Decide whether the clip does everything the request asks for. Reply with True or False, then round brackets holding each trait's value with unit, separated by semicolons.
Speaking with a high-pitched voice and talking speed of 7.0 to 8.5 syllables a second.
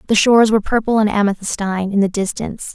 True (210 Hz; 7.1 syllables/s)